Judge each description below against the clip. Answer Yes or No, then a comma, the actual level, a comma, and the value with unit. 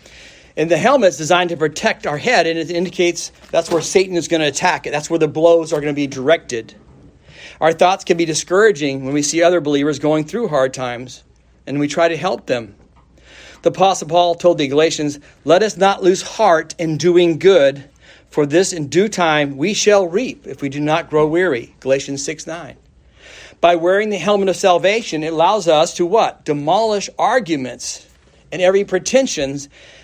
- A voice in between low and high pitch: Yes, medium, 165 Hz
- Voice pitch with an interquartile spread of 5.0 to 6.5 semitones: No, average, 4.0 semitones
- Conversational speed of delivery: Yes, average, 190 wpm